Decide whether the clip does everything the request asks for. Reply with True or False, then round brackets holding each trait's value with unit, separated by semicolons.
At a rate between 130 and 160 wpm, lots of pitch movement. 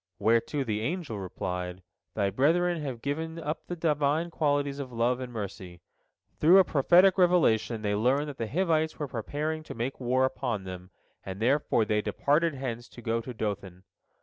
False (175 wpm; 6.0 semitones)